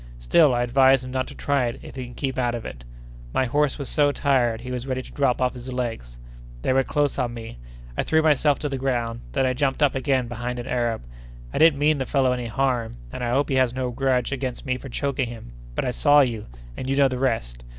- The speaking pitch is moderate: No, low, 130 Hz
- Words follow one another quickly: Yes, fast, 250 wpm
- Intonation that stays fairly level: Yes, narrow, 2.2 semitones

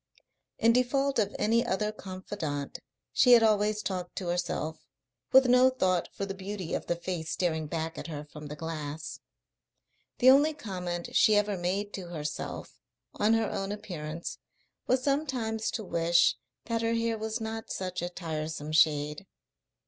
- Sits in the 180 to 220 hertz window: Yes, high, 190 Hz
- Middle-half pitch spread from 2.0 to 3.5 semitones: No, average, 5.3 semitones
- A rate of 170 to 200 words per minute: No, average, 160 wpm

